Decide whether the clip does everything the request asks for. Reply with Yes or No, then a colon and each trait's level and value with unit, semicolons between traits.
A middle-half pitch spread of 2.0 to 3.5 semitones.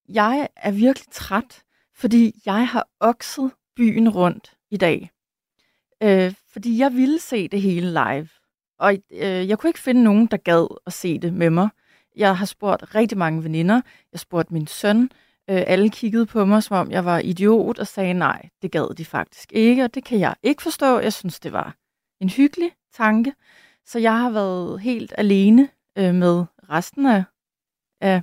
No: average, 4.5 semitones